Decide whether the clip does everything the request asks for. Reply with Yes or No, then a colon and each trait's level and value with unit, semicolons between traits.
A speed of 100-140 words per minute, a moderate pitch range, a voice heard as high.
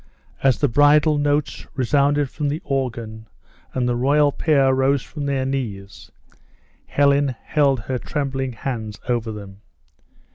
No: slow, 135 wpm; average, 3.2 semitones; low, 135 Hz